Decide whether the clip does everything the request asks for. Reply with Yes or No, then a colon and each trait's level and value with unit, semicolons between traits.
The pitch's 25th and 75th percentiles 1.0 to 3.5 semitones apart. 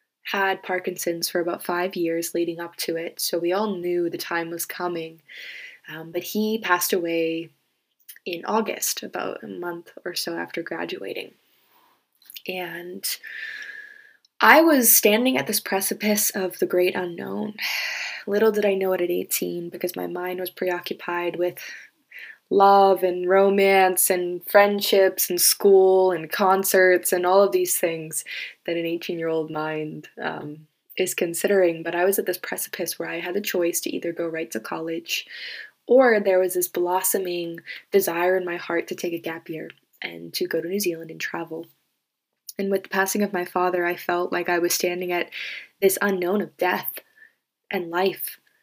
Yes: narrow, 2.5 semitones